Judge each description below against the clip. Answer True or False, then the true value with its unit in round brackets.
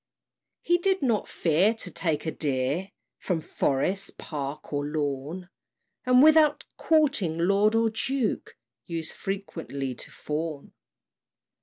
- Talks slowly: True (120 wpm)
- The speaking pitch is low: False (180 Hz)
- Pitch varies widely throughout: True (7.1 semitones)